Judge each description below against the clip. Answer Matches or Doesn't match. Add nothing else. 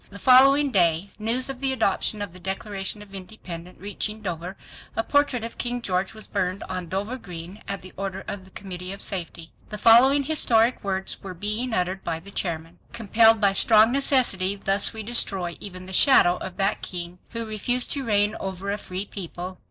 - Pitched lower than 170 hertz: Doesn't match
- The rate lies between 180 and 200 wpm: Matches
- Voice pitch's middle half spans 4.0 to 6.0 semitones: Doesn't match